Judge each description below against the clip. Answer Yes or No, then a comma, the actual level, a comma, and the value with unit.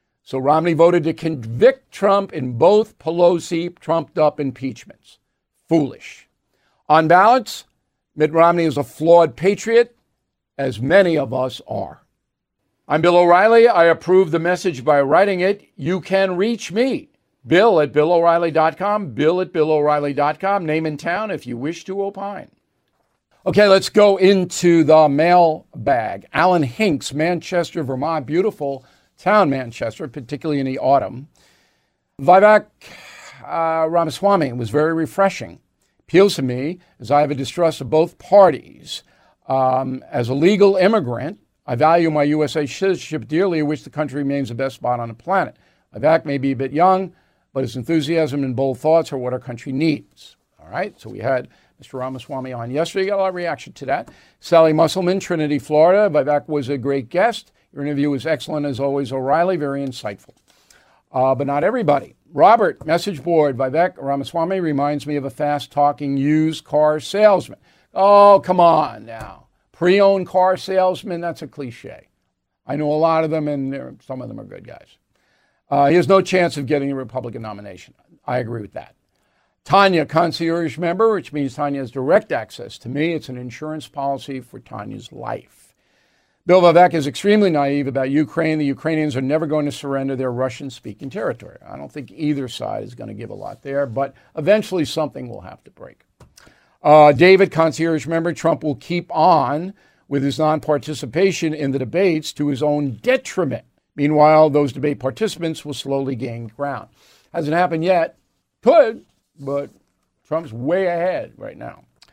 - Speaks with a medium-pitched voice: Yes, medium, 155 Hz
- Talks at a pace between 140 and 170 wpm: Yes, average, 165 wpm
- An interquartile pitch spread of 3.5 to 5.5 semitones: Yes, average, 4.0 semitones